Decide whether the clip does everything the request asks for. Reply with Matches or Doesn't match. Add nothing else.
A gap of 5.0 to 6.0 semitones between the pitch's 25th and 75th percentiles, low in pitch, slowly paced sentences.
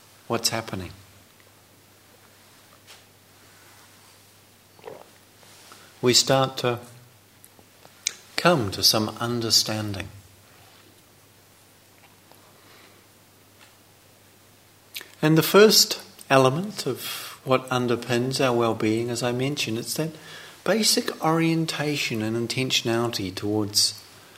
Doesn't match